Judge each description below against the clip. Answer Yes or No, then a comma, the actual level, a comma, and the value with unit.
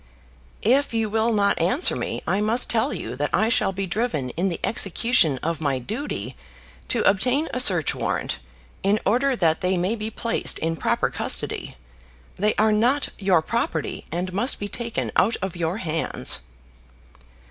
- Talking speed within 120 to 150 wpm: No, average, 170 wpm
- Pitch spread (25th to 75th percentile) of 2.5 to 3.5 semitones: No, average, 5.1 semitones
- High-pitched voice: Yes, high, 205 Hz